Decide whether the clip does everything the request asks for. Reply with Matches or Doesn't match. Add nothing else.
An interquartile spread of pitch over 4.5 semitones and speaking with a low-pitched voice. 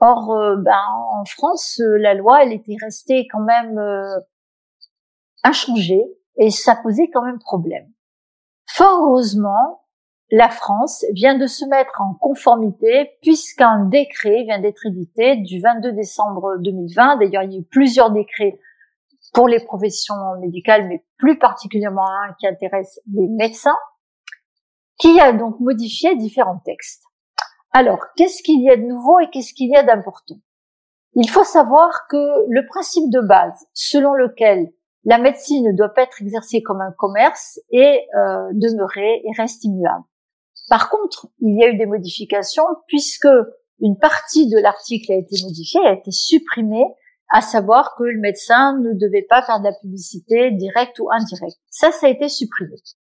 Doesn't match